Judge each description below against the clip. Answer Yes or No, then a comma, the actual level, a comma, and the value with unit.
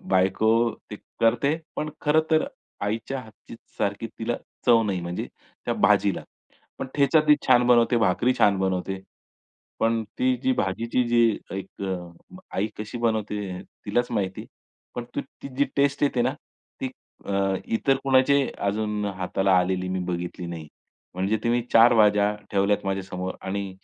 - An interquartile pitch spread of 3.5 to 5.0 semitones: Yes, average, 4.2 semitones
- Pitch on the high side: No, low, 105 Hz